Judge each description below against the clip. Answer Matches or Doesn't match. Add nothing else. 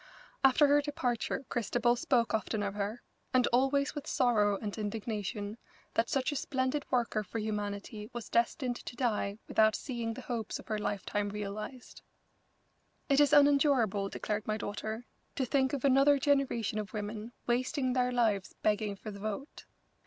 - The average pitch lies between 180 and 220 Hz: Doesn't match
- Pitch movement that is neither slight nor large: Matches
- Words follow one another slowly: Doesn't match